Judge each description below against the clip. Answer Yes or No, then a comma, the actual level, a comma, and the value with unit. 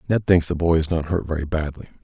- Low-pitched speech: Yes, very low, 85 Hz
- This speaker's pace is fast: Yes, fast, 265 wpm